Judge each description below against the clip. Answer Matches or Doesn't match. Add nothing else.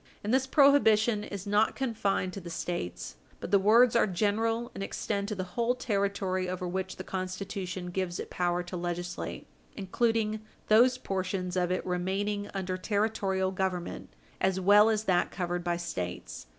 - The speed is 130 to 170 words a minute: Matches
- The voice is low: Doesn't match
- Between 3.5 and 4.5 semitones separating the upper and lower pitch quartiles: Doesn't match